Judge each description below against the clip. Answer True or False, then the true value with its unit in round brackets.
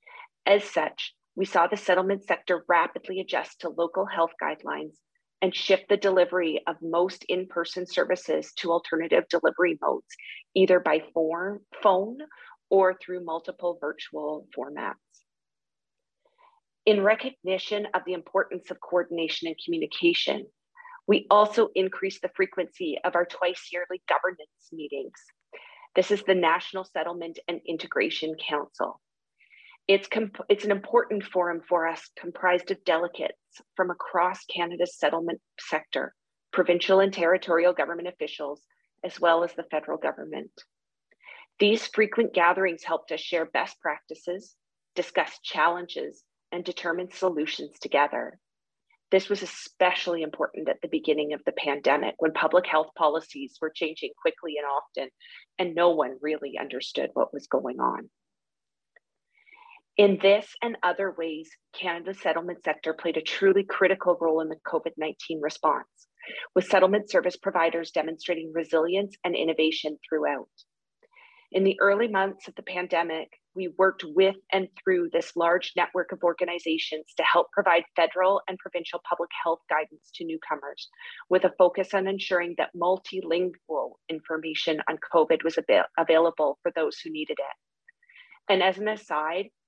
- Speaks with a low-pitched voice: False (180 Hz)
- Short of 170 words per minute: True (140 wpm)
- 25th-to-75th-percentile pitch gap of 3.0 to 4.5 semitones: True (3.3 semitones)